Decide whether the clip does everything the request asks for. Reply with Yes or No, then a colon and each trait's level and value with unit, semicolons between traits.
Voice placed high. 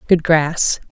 No: medium, 160 Hz